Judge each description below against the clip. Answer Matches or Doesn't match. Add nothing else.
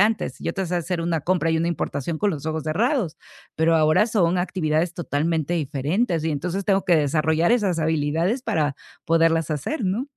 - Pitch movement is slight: Doesn't match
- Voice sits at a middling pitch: Matches